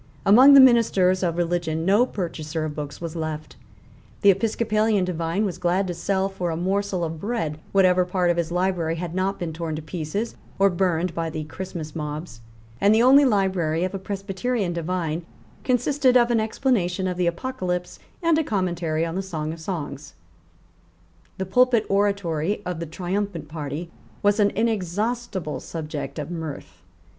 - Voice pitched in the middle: Yes, medium, 180 Hz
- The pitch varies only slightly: No, average, 3.7 semitones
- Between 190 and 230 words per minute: No, average, 170 wpm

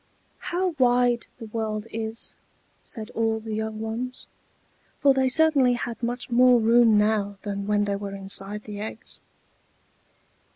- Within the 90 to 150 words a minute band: Yes, average, 140 wpm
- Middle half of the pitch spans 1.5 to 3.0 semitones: Yes, average, 2.7 semitones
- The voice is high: Yes, high, 225 Hz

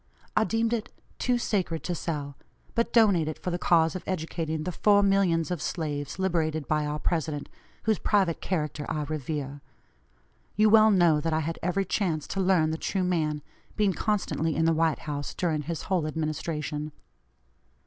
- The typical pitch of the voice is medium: Yes, medium, 165 Hz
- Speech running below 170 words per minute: No, average, 175 wpm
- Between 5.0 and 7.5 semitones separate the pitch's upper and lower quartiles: No, average, 3.7 semitones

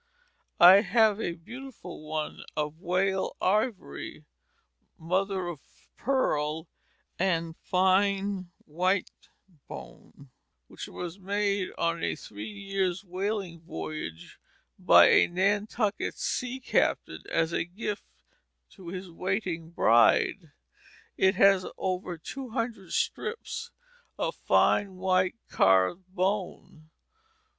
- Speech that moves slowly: Yes, slow, 100 wpm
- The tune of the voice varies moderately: Yes, average, 3.2 semitones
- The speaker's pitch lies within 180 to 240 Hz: Yes, medium, 185 Hz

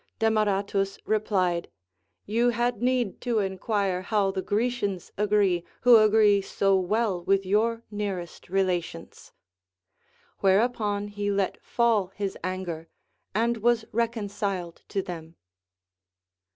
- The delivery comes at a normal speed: No, slow, 110 wpm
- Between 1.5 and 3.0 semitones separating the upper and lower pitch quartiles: Yes, average, 2.7 semitones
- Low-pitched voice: No, high, 205 Hz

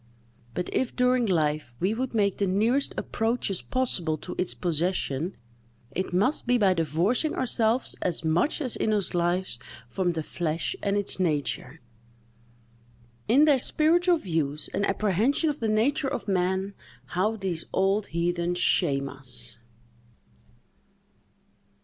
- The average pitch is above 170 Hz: Yes, high, 190 Hz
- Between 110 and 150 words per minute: Yes, slow, 135 wpm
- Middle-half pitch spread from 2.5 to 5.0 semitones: No, wide, 5.5 semitones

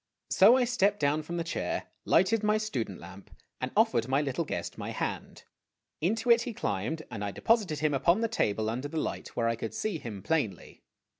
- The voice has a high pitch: No, medium, 155 Hz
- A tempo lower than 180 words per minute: No, fast, 205 wpm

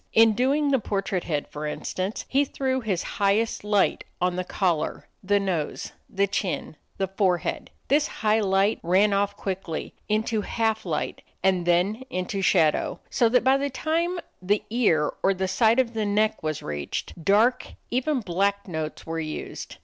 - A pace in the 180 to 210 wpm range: No, average, 165 wpm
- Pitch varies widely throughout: No, average, 3.8 semitones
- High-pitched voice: Yes, high, 200 Hz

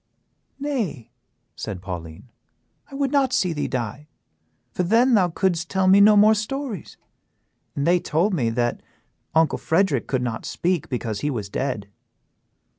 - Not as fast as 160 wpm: Yes, average, 150 wpm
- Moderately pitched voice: Yes, medium, 170 Hz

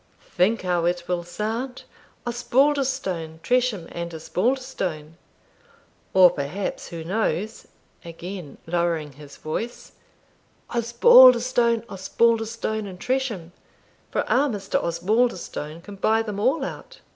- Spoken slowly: Yes, slow, 105 wpm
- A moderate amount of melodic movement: No, wide, 5.8 semitones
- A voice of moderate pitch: No, high, 200 Hz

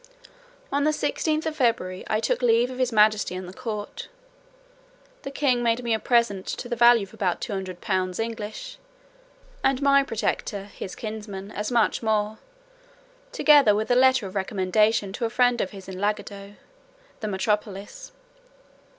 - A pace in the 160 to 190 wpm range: Yes, average, 170 wpm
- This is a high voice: Yes, high, 220 Hz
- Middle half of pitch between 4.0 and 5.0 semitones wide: No, average, 3.6 semitones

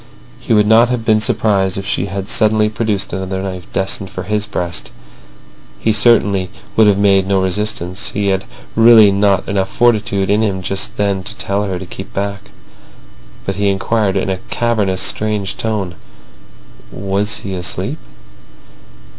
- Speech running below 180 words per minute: Yes, average, 160 wpm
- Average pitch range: No, narrow, 1.9 semitones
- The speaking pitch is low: Yes, low, 100 Hz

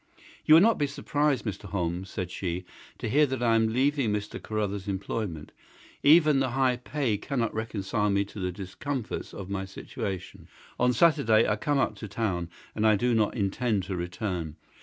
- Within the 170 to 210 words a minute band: Yes, average, 180 wpm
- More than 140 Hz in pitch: No, low, 110 Hz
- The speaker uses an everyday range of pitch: Yes, average, 5.0 semitones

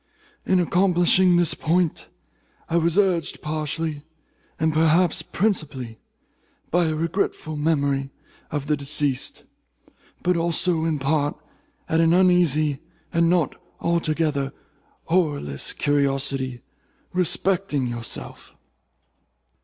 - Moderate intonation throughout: Yes, average, 3.3 semitones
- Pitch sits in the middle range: Yes, medium, 160 Hz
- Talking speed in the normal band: No, slow, 100 wpm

